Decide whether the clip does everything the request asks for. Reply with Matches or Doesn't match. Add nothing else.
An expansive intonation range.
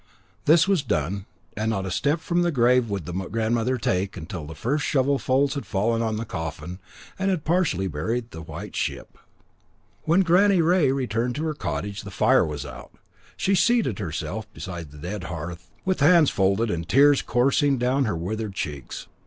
Matches